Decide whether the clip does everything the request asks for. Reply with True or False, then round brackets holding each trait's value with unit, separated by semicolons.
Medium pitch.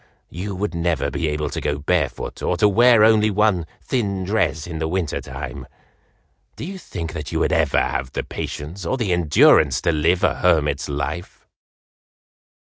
False (85 Hz)